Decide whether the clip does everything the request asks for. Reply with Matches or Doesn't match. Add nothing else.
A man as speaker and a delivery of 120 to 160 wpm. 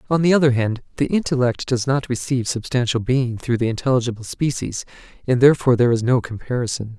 Doesn't match